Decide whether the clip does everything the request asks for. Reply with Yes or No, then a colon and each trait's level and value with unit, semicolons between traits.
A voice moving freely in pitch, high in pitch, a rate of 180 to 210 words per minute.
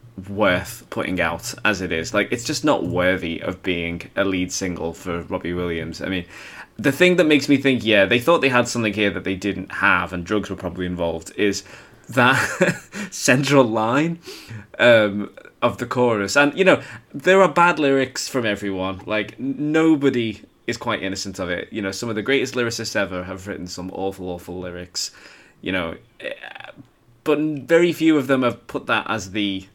No: wide, 6.3 semitones; low, 105 Hz; average, 190 wpm